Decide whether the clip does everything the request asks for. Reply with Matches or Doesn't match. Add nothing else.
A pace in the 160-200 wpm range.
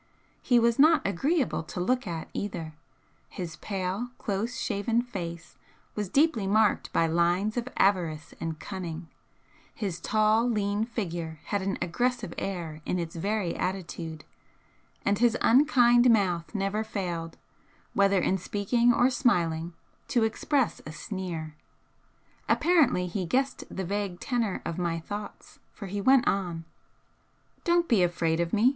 Doesn't match